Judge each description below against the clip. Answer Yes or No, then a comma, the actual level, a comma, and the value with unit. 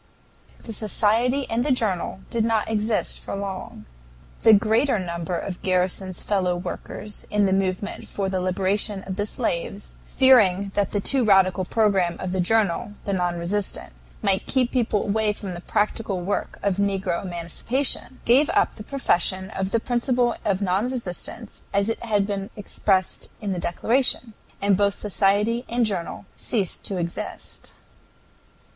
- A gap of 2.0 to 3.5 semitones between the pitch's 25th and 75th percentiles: Yes, average, 3.1 semitones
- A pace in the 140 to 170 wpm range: Yes, average, 155 wpm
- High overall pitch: Yes, high, 200 Hz